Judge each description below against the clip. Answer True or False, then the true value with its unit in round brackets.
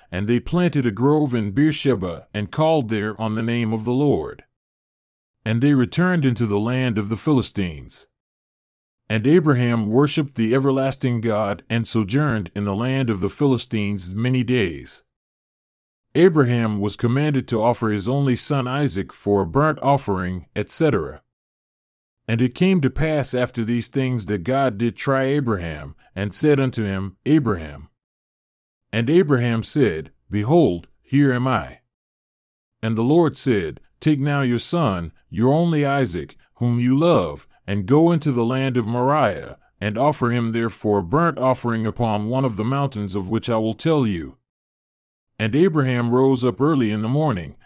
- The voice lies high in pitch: False (120 Hz)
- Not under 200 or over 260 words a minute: False (160 wpm)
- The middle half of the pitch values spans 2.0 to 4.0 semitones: False (4.5 semitones)